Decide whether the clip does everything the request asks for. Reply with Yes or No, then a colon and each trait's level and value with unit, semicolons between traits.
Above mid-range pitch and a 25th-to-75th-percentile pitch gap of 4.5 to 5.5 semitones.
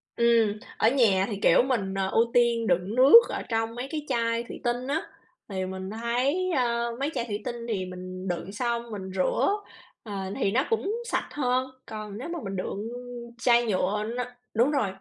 No: high, 230 Hz; average, 3.9 semitones